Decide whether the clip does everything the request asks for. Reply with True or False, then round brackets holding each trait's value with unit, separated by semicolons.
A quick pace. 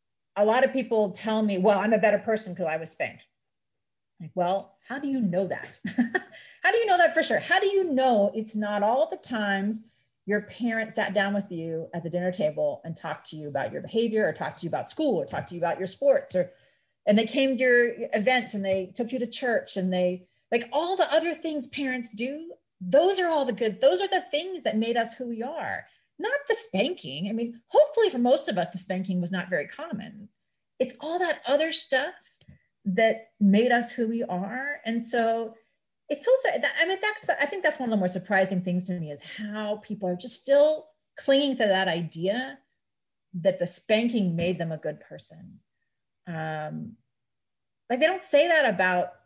True (215 wpm)